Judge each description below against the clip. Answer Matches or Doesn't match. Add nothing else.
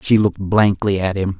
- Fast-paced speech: Matches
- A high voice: Doesn't match